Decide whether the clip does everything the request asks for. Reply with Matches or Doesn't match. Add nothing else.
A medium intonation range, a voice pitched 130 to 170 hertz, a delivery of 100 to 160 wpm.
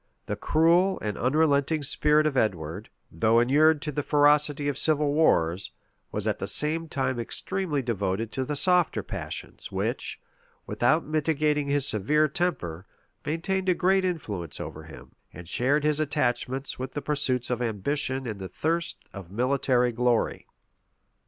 Matches